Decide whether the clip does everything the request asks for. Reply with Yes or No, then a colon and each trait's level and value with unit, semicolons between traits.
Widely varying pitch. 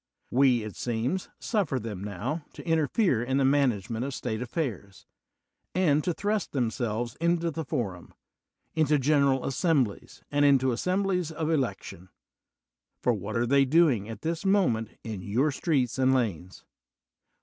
Yes: wide, 6.0 semitones